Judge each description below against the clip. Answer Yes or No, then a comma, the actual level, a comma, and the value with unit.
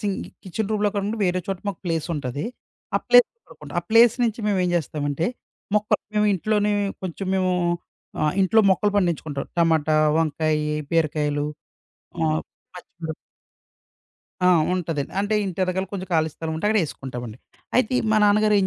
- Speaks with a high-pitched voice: No, medium, 180 Hz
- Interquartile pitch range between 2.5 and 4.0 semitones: No, average, 4.8 semitones